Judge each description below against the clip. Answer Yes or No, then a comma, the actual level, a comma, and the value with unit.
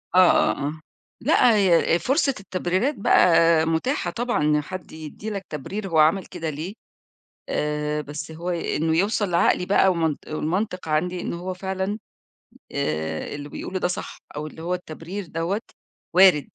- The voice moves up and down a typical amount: Yes, average, 3.5 semitones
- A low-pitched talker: No, medium, 175 Hz